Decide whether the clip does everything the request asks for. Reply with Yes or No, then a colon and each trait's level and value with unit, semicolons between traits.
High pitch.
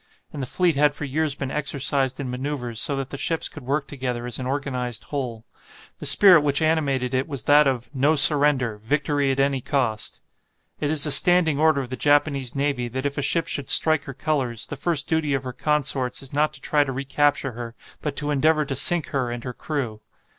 No: medium, 140 Hz